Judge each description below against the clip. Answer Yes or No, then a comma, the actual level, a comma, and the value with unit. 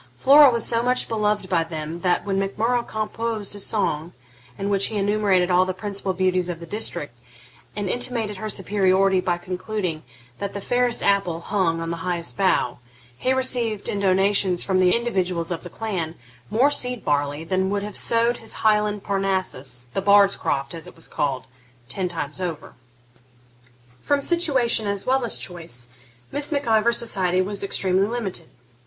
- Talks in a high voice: Yes, high, 195 Hz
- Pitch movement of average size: Yes, average, 3.6 semitones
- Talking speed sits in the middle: Yes, average, 175 wpm